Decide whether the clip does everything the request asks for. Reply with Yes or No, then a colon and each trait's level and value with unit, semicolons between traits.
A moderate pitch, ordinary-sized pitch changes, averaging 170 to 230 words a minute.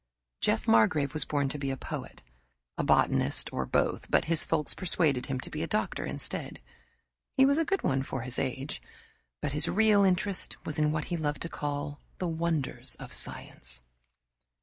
Yes: medium, 150 Hz; average, 3.8 semitones; average, 185 wpm